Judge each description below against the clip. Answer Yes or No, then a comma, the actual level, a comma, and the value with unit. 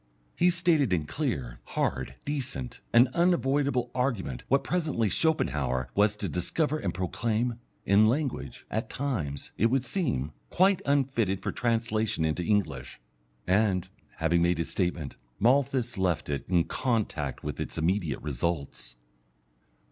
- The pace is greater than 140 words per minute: No, slow, 135 wpm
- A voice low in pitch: Yes, low, 110 Hz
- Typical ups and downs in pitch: No, wide, 7.8 semitones